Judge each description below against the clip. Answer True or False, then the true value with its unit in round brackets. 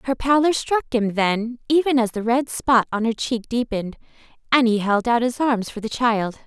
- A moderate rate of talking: False (215 wpm)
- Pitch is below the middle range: False (235 Hz)